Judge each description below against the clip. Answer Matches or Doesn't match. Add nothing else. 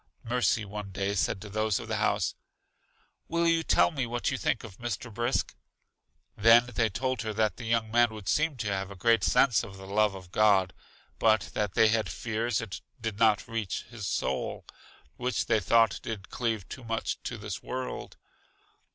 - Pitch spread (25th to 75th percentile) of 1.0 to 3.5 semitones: Matches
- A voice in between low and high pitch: Doesn't match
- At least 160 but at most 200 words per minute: Matches